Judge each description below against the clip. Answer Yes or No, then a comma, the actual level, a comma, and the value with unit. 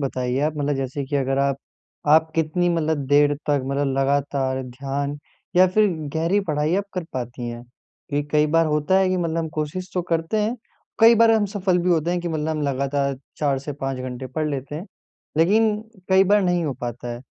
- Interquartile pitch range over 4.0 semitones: Yes, average, 4.4 semitones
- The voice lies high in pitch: No, medium, 150 Hz